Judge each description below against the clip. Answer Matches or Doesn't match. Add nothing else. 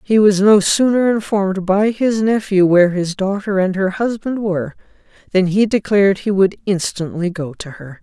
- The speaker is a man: Doesn't match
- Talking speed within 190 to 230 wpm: Doesn't match